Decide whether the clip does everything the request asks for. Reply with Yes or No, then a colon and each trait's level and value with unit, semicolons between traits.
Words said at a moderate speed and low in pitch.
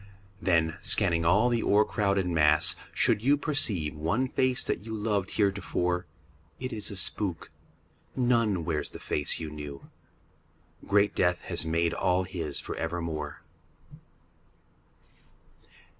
No: slow, 125 wpm; very low, 90 Hz